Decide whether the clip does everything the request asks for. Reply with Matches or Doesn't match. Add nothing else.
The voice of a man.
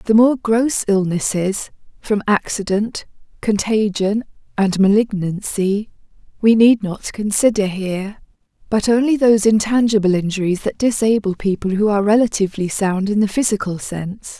Doesn't match